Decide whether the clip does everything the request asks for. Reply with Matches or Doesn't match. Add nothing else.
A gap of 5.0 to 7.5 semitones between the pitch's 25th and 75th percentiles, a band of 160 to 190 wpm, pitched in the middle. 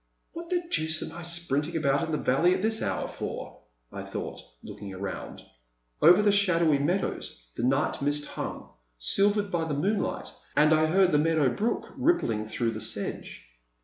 Matches